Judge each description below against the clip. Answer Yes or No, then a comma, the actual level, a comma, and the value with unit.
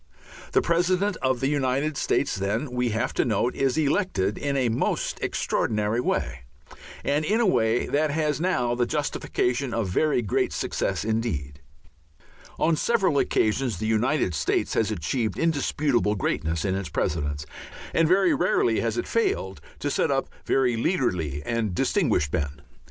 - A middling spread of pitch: No, wide, 6.5 semitones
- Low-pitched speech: Yes, low, 125 Hz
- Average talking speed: Yes, average, 155 wpm